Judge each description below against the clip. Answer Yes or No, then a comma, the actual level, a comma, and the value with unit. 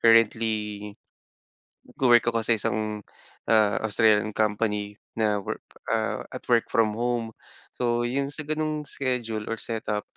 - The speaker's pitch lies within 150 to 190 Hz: No, low, 115 Hz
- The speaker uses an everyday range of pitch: No, narrow, 2.1 semitones